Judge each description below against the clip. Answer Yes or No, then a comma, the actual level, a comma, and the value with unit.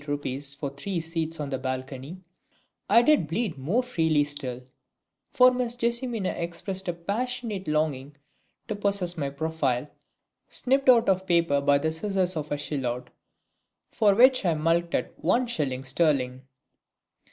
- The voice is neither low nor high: Yes, medium, 165 Hz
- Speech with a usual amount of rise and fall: No, wide, 6.4 semitones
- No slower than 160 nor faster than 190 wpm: No, average, 140 wpm